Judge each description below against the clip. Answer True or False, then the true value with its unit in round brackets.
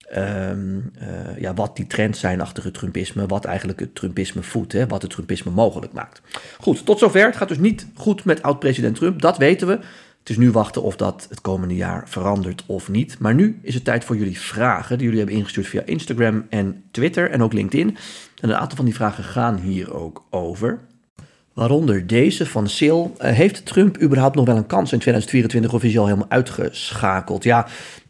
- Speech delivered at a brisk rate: True (205 wpm)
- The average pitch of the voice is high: False (115 Hz)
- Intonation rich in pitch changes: True (6.0 semitones)